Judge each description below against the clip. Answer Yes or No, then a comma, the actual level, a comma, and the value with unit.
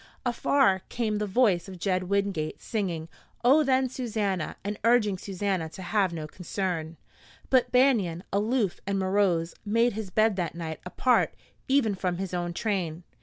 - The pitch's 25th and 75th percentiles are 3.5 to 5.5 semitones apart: Yes, average, 4.2 semitones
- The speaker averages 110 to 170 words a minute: Yes, average, 155 wpm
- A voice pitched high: Yes, high, 195 Hz